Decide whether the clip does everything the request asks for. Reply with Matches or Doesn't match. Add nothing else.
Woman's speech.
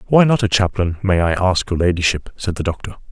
Doesn't match